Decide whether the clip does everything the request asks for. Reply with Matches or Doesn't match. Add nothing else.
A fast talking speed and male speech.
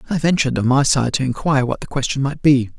Matches